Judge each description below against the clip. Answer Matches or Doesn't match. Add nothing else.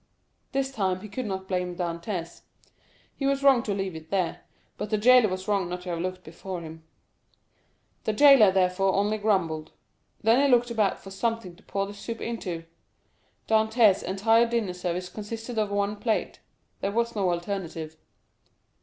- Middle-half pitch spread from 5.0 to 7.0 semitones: Doesn't match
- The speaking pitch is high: Matches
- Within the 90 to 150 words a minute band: Doesn't match